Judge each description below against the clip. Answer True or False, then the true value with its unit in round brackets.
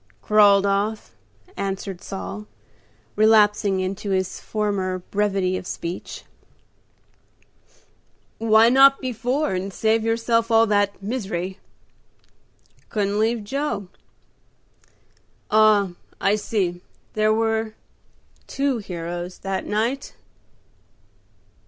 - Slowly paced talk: True (90 wpm)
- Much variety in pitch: False (2.5 semitones)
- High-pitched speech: True (210 Hz)